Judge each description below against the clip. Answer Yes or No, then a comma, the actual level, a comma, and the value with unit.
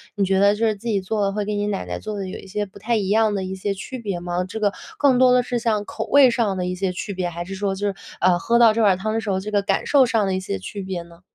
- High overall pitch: Yes, high, 200 Hz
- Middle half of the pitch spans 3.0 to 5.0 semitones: No, narrow, 2.6 semitones